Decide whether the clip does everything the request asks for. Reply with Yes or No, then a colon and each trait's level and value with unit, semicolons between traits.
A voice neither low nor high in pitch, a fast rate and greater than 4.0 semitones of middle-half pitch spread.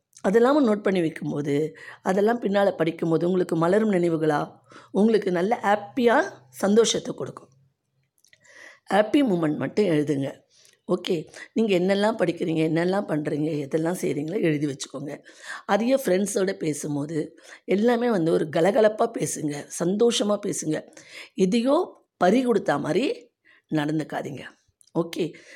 No: medium, 180 Hz; average, 105 wpm; wide, 5.4 semitones